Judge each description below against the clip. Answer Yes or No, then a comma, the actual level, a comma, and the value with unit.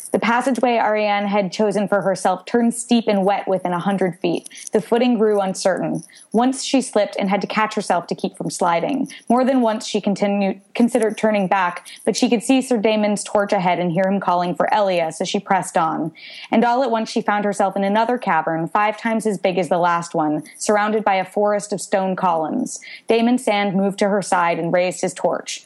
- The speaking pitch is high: Yes, high, 205 Hz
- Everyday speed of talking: No, fast, 215 wpm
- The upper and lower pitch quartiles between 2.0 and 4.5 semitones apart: Yes, average, 2.9 semitones